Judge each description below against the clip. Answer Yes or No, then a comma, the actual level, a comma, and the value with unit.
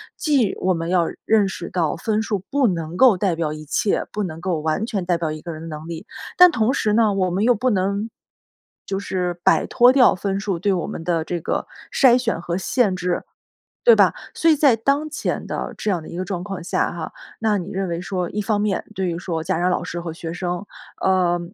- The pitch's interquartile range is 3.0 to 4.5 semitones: Yes, average, 3.8 semitones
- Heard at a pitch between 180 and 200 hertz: Yes, medium, 185 Hz